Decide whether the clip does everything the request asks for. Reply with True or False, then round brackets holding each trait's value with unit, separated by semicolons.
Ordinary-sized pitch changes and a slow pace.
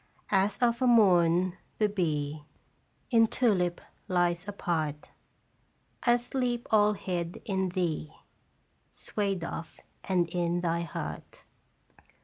True (3.6 semitones; 110 wpm)